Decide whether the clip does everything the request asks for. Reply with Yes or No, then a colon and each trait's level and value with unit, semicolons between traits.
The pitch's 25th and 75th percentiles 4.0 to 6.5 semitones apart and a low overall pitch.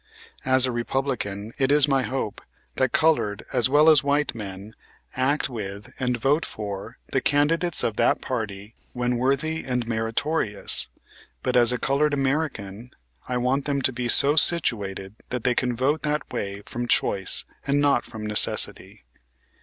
Yes: average, 4.3 semitones; low, 125 Hz